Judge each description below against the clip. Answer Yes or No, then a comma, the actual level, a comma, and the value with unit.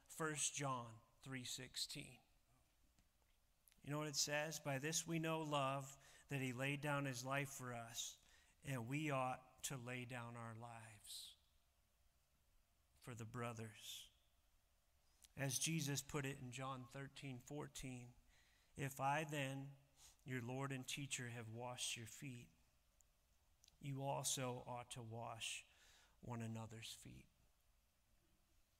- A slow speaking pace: Yes, slow, 120 wpm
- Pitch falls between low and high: No, low, 125 Hz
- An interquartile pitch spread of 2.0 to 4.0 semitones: No, average, 5.3 semitones